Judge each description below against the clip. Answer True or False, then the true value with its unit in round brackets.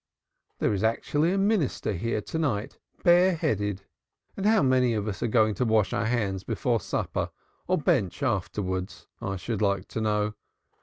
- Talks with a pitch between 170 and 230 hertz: False (110 Hz)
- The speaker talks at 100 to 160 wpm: False (170 wpm)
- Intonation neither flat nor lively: False (6.0 semitones)